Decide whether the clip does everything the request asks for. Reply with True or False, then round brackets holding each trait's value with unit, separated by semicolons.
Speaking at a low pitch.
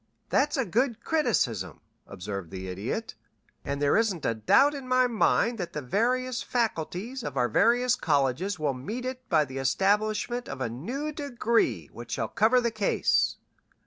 False (215 Hz)